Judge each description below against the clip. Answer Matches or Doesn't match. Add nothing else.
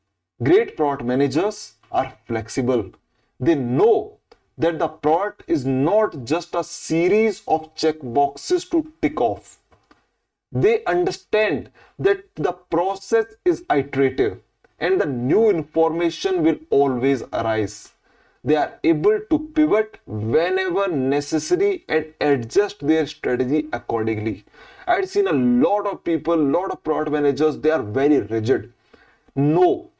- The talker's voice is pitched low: Doesn't match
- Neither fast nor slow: Doesn't match